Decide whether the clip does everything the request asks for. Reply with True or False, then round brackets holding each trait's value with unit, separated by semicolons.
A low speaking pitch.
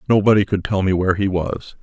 True (95 Hz)